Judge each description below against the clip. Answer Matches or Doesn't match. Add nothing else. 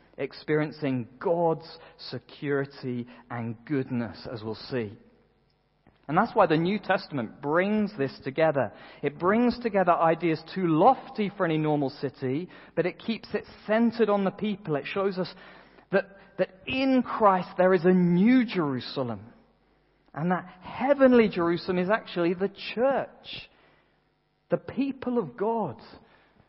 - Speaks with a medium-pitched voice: Matches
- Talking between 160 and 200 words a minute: Doesn't match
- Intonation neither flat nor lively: Doesn't match